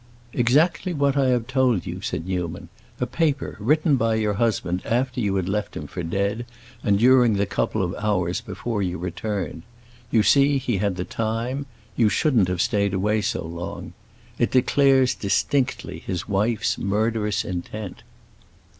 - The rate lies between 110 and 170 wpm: Yes, average, 160 wpm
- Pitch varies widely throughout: No, average, 4.6 semitones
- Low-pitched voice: Yes, low, 110 Hz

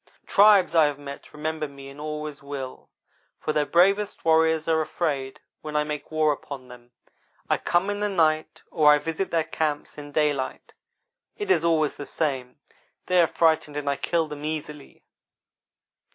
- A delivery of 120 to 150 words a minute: No, average, 170 wpm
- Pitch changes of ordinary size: No, narrow, 2.0 semitones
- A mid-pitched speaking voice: Yes, medium, 155 Hz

